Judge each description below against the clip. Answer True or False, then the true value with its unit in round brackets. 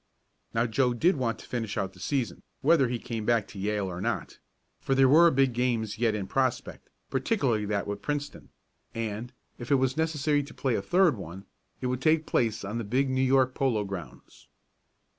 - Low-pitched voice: True (125 Hz)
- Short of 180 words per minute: False (200 wpm)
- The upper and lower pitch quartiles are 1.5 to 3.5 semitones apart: False (4.0 semitones)